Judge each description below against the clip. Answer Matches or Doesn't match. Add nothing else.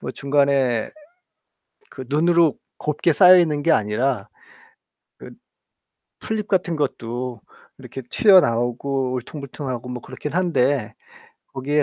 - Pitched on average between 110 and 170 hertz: Matches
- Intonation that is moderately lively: Matches